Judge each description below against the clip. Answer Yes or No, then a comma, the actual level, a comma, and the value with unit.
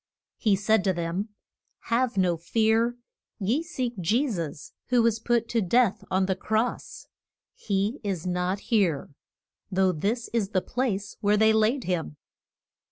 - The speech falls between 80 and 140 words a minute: No, average, 150 wpm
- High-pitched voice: Yes, high, 210 Hz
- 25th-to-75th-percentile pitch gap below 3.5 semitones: No, average, 3.8 semitones